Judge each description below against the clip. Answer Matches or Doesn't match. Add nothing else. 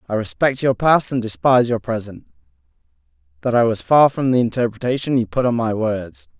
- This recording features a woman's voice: Doesn't match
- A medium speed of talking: Matches